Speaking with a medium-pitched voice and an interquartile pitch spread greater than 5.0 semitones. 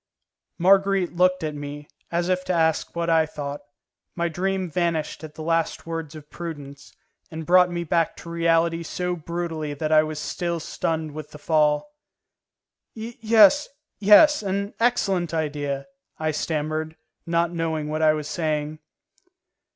No: medium, 165 Hz; narrow, 2.5 semitones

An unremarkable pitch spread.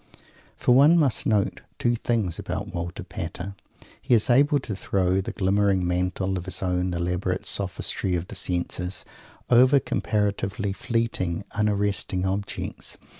Yes: average, 3.0 semitones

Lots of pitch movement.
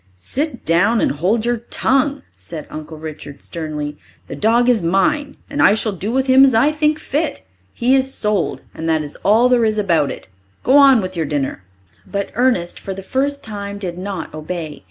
Yes: wide, 7.7 semitones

